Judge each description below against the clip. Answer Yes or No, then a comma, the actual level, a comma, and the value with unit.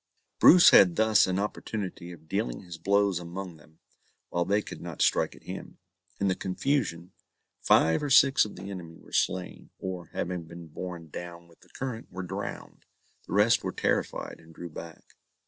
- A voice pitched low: Yes, very low, 90 Hz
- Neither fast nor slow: Yes, average, 180 wpm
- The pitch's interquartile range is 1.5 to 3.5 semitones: Yes, average, 3.1 semitones